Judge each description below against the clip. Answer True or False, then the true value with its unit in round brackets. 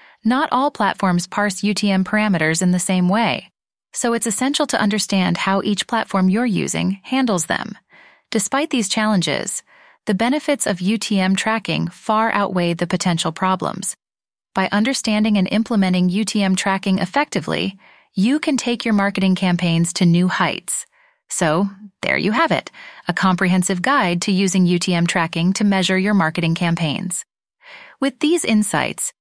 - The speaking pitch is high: True (200 Hz)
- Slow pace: False (145 wpm)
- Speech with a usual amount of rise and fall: True (3.5 semitones)